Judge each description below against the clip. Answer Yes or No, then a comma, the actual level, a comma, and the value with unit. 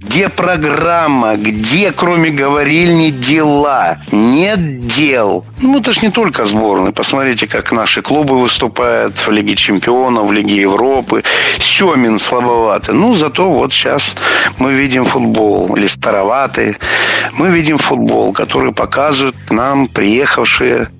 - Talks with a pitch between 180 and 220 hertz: No, medium, 140 Hz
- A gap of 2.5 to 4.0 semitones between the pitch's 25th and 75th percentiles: No, wide, 5.6 semitones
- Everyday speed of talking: Yes, average, 125 wpm